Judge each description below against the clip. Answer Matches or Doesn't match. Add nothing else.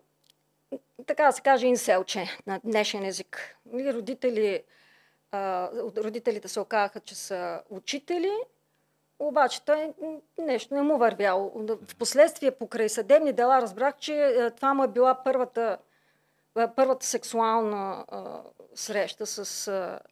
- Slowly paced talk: Matches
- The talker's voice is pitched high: Matches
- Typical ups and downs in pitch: Matches